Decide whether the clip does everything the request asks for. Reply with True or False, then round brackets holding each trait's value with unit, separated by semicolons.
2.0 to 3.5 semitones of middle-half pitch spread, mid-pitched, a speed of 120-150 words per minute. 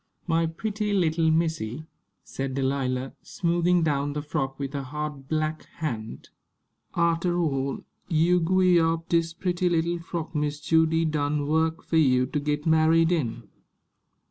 True (2.6 semitones; 160 Hz; 145 wpm)